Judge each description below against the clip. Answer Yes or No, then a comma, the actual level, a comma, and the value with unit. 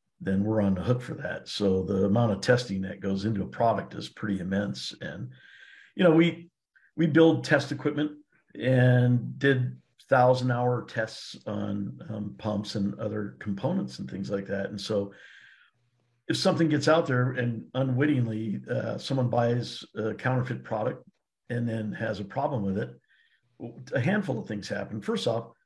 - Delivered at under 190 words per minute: Yes, average, 170 wpm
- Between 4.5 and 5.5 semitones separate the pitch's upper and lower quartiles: Yes, average, 4.9 semitones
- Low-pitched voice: Yes, low, 120 Hz